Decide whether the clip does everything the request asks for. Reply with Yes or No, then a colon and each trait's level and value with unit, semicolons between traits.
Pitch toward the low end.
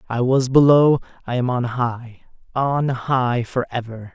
Yes: low, 125 Hz